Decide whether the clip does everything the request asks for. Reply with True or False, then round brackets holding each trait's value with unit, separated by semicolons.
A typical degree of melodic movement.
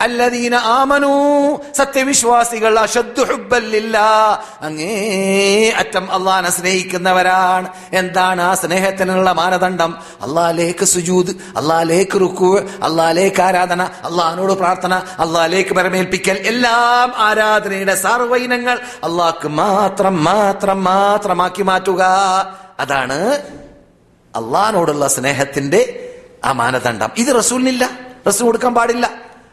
True (4.3 semitones)